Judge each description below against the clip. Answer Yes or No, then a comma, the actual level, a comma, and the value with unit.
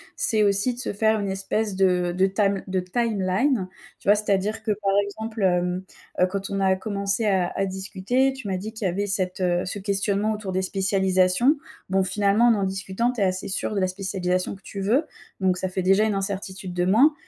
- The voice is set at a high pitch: Yes, high, 195 Hz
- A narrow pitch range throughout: Yes, narrow, 2.1 semitones